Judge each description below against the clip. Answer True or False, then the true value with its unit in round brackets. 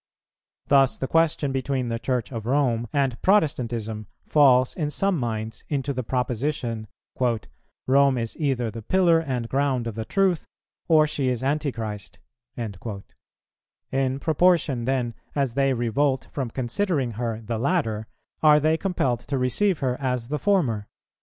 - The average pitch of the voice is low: True (130 Hz)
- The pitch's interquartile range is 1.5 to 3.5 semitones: False (4.0 semitones)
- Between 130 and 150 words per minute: True (145 wpm)